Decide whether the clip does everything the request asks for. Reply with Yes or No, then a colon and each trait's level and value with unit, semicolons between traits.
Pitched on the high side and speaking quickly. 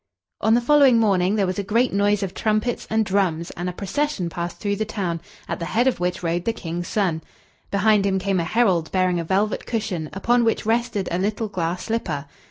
Yes: high, 200 Hz; fast, 215 wpm